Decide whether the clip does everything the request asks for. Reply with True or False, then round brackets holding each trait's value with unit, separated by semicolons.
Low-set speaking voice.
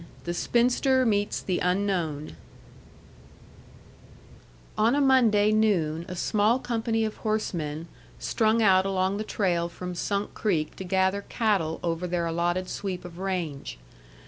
False (190 Hz)